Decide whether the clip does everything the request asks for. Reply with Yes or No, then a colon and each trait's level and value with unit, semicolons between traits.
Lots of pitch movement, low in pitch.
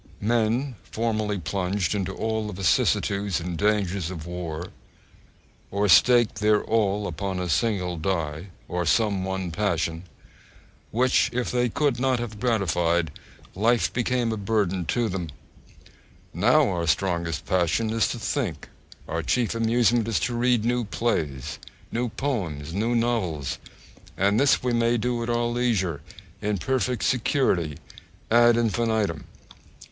No: average, 5.0 semitones; low, 105 Hz